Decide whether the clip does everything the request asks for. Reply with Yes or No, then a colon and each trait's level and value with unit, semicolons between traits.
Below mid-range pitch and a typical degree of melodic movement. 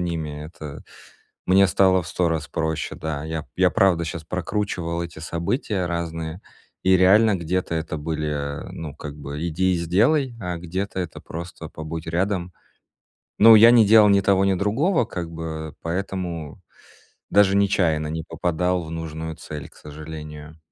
Yes: very low, 85 Hz; average, 3.1 semitones